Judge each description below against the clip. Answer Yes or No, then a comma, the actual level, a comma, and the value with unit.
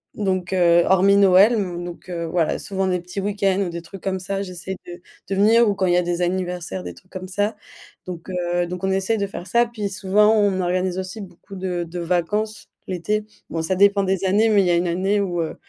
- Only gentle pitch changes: Yes, narrow, 2.2 semitones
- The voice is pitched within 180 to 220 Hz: Yes, medium, 185 Hz